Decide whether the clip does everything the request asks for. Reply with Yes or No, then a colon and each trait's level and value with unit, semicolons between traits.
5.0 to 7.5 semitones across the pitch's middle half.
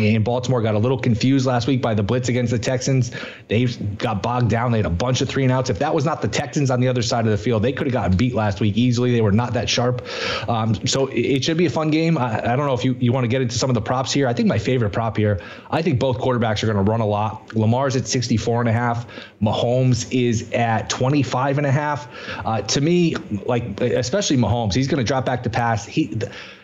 No: average, 2.8 semitones